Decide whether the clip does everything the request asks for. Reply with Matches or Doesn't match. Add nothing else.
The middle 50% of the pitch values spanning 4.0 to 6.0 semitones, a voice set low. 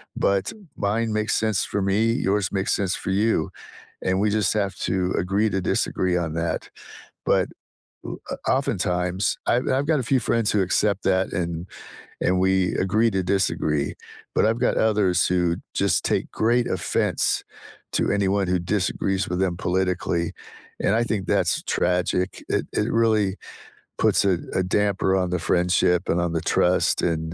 Doesn't match